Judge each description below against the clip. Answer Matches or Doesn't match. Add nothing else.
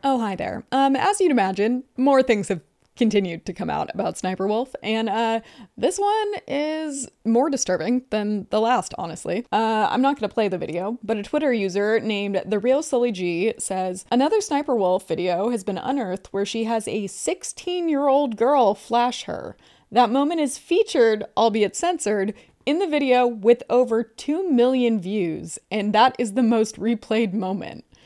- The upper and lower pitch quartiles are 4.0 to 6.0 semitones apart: Matches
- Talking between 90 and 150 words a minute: Doesn't match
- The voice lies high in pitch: Matches